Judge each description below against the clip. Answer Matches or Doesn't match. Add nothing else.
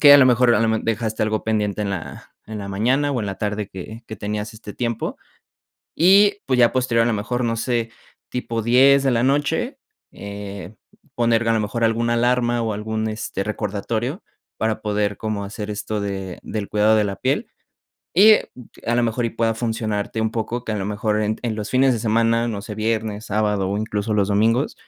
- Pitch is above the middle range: Doesn't match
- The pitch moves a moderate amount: Doesn't match